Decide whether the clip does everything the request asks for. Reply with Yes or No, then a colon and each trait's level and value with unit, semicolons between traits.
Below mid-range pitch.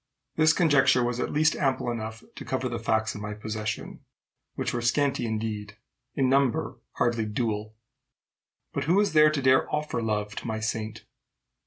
Yes: low, 120 Hz